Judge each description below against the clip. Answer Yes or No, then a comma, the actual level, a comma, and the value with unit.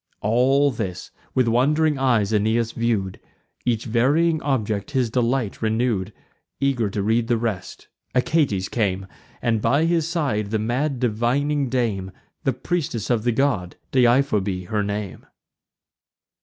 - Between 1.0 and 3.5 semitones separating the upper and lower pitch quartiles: No, average, 4.1 semitones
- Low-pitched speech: Yes, low, 120 Hz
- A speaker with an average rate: No, slow, 130 wpm